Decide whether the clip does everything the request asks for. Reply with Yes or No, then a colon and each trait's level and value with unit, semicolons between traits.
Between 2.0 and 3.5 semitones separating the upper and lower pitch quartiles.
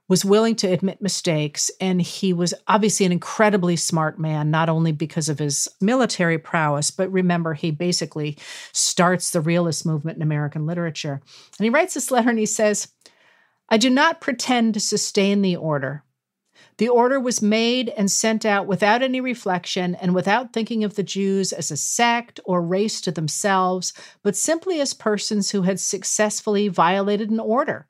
No: average, 4.6 semitones